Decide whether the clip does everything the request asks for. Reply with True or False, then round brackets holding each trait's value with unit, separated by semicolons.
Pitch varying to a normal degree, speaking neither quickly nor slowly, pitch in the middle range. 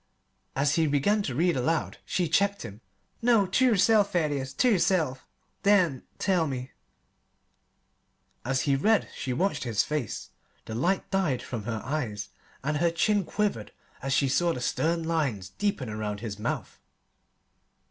False (7.1 semitones; 150 wpm; 155 Hz)